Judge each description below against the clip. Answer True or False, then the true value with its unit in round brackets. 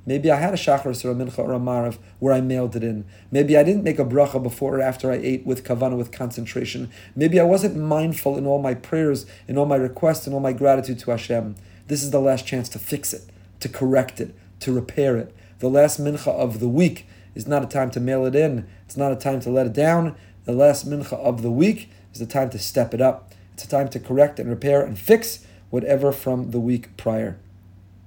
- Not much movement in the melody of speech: False (3.5 semitones)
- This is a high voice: False (130 Hz)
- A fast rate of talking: True (235 wpm)